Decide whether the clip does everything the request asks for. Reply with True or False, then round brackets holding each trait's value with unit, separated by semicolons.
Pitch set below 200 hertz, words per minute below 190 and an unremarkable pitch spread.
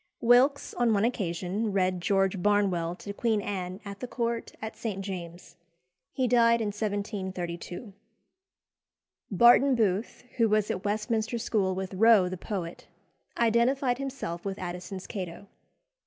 False (205 Hz; 135 wpm; 3.8 semitones)